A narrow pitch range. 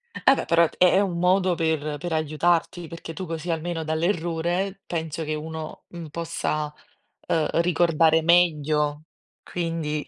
Yes: narrow, 1.9 semitones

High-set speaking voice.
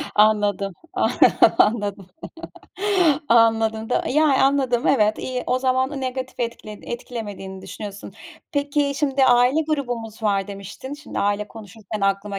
Yes: high, 230 Hz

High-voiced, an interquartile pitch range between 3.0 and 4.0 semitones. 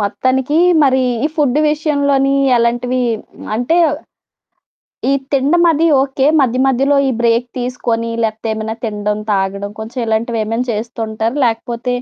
Yes: high, 240 Hz; average, 3.3 semitones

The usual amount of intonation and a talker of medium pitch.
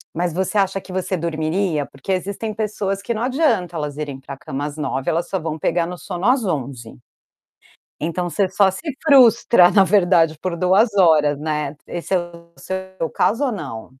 Yes: average, 4.2 semitones; medium, 175 Hz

